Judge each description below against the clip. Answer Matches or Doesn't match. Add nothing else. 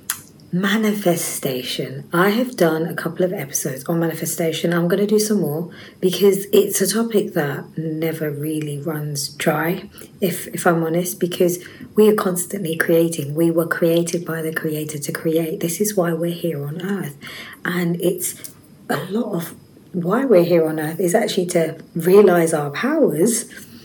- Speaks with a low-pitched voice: Doesn't match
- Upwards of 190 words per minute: Doesn't match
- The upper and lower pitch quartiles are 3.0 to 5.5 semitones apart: Doesn't match